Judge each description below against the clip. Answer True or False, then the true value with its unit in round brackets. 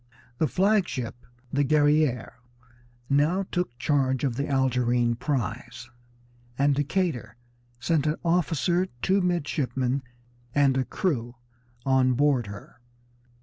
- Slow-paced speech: True (110 wpm)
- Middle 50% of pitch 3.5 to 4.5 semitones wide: True (4.1 semitones)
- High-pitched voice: False (140 Hz)